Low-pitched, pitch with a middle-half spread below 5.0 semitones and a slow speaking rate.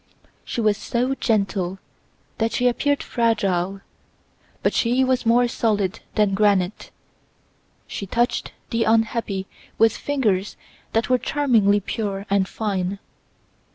No: high, 220 Hz; average, 3.3 semitones; slow, 120 wpm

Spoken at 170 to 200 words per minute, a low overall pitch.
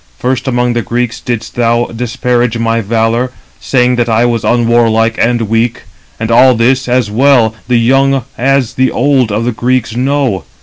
Yes: average, 175 wpm; low, 120 Hz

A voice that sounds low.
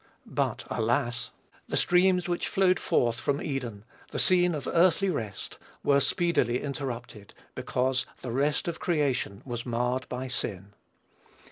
Yes: low, 130 Hz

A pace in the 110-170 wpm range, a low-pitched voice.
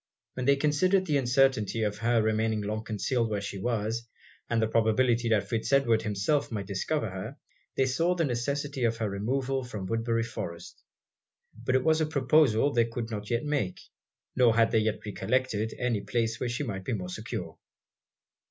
No: average, 180 wpm; low, 115 Hz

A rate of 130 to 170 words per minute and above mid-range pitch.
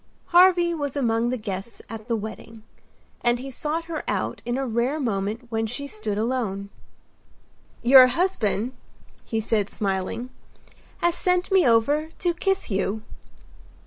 Yes: average, 145 wpm; high, 240 Hz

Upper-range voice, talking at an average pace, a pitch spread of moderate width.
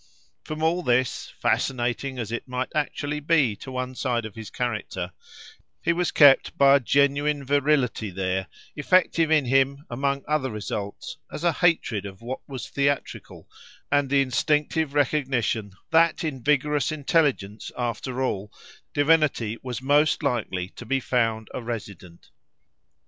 No: low, 135 Hz; average, 145 wpm; average, 4.0 semitones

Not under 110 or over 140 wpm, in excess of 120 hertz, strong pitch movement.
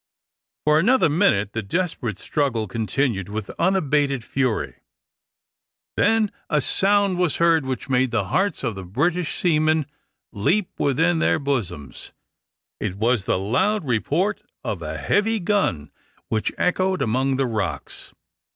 Yes: slow, 135 wpm; medium, 140 Hz; wide, 8.1 semitones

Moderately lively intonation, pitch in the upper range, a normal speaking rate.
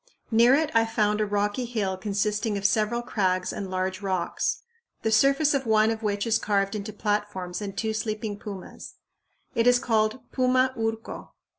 No: narrow, 2.2 semitones; high, 215 Hz; average, 170 wpm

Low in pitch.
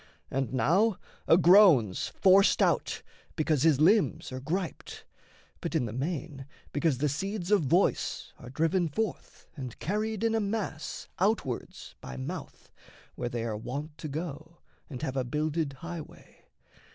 No: medium, 155 Hz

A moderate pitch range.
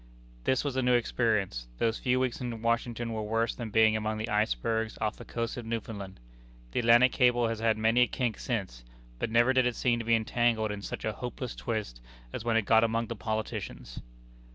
No: narrow, 1.7 semitones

